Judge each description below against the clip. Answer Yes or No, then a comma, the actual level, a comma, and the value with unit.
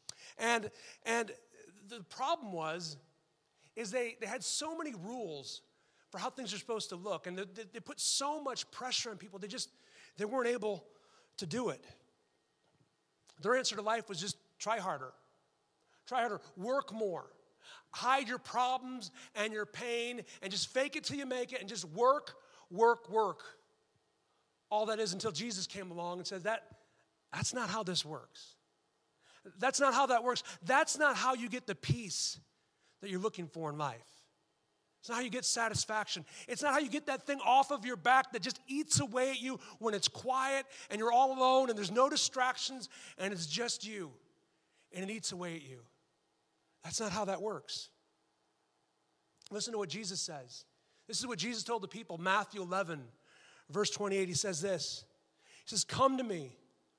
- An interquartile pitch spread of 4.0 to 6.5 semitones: Yes, average, 5.1 semitones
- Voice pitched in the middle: No, high, 220 Hz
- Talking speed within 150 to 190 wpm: Yes, average, 180 wpm